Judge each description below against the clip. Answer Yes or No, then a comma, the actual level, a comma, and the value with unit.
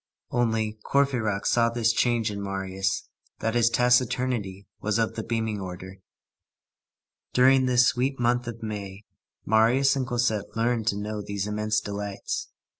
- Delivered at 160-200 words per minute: No, average, 140 wpm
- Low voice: Yes, low, 110 Hz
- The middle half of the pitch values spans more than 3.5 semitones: No, average, 3.0 semitones